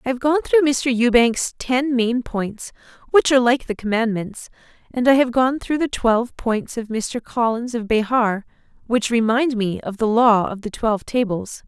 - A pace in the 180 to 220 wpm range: Yes, average, 190 wpm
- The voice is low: No, high, 235 Hz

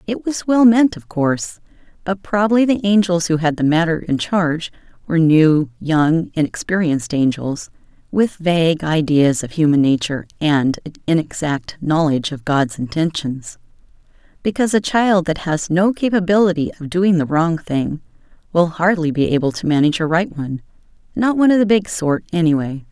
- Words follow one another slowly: No, average, 160 wpm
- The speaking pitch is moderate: Yes, medium, 165 Hz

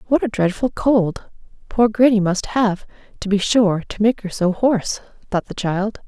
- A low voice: No, high, 210 Hz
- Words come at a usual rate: Yes, average, 190 wpm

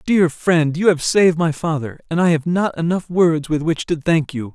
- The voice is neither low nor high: Yes, medium, 165 Hz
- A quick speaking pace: Yes, fast, 235 wpm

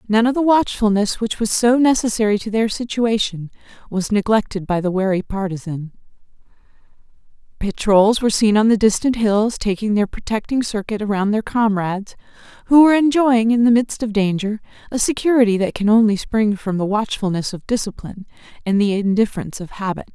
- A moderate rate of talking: Yes, average, 165 wpm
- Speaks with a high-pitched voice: Yes, high, 215 Hz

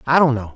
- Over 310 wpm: Yes, fast, 320 wpm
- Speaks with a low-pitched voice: Yes, low, 130 Hz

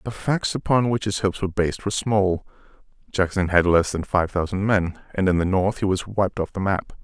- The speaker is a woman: No, male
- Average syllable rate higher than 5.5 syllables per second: Yes, 5.7 syllables/s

